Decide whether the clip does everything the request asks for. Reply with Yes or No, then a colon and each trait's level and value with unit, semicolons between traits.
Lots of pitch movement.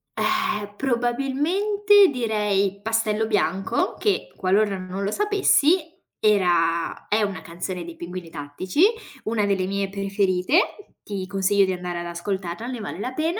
Yes: wide, 5.8 semitones